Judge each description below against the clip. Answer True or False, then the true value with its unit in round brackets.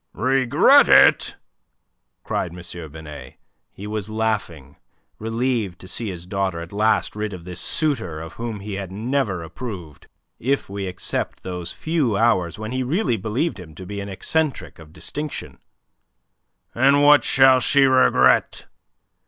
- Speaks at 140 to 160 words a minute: True (145 wpm)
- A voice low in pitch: True (105 Hz)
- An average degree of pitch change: False (6.1 semitones)